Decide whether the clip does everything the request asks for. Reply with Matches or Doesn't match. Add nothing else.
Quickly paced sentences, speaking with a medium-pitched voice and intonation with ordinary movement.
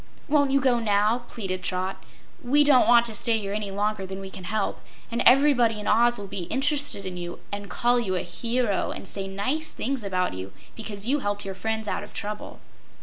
Doesn't match